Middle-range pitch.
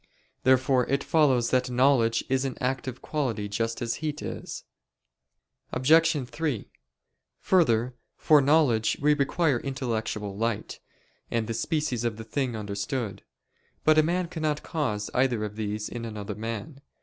No: low, 125 Hz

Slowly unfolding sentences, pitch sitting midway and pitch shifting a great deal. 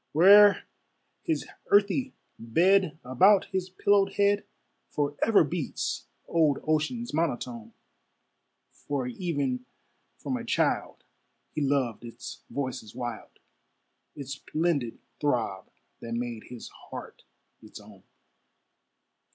Yes: slow, 100 wpm; medium, 145 Hz; wide, 7.3 semitones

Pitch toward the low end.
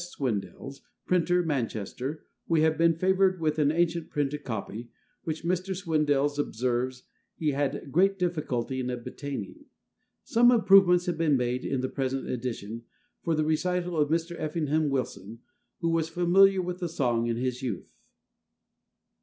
No: medium, 150 Hz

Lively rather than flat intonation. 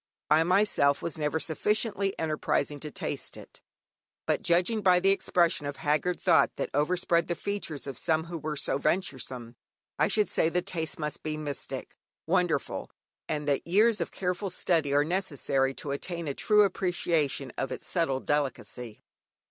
No: average, 3.9 semitones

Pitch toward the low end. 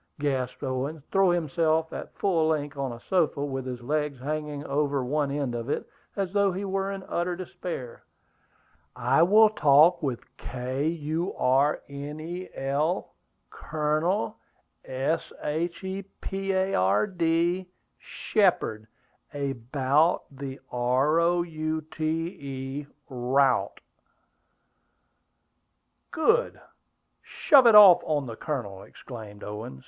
No: medium, 150 Hz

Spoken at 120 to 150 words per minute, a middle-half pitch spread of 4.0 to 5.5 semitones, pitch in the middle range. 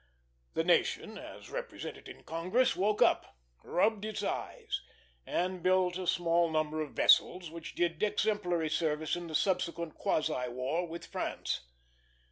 No: average, 140 wpm; average, 2.7 semitones; medium, 170 Hz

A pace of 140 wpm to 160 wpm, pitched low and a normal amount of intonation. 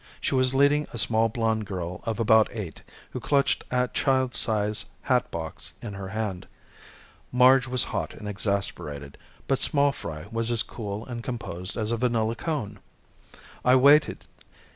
Yes: average, 155 wpm; low, 115 Hz; average, 3.8 semitones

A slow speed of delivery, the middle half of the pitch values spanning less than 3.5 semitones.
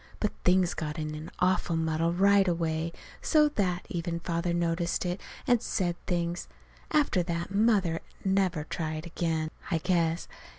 No: average, 145 wpm; narrow, 2.4 semitones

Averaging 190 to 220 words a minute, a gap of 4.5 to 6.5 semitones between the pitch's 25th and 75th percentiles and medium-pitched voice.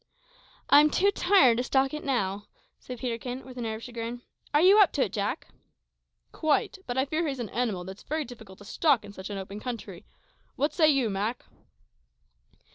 No: average, 195 wpm; average, 5.1 semitones; very high, 250 Hz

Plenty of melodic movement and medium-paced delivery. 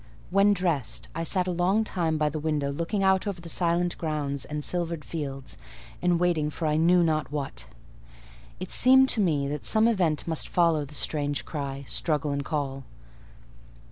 No: average, 3.4 semitones; average, 175 wpm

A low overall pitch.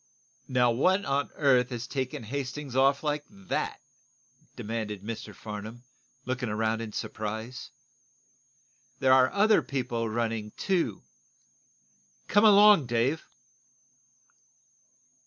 Yes: low, 125 Hz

